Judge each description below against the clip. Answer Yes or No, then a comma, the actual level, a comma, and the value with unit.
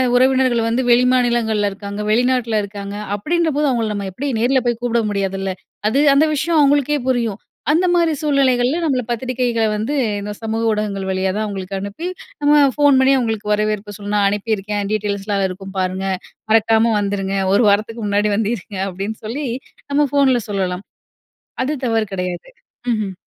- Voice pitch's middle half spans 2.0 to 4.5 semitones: Yes, average, 4.2 semitones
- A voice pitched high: Yes, high, 220 Hz